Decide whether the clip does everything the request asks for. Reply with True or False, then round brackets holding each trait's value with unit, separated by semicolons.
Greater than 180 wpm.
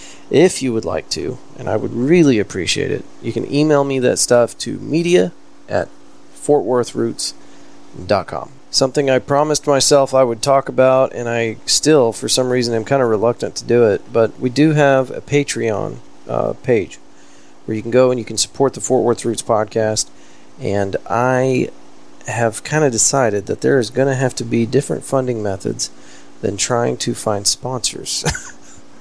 False (175 wpm)